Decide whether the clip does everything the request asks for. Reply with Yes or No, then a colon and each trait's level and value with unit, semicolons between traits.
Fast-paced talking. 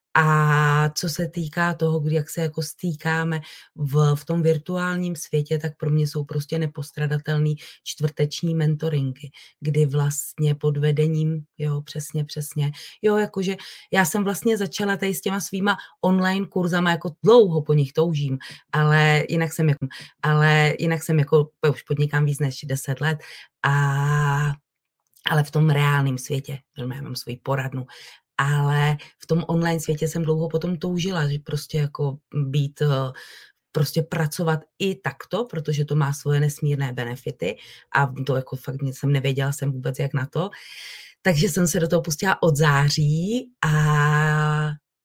No: average, 150 wpm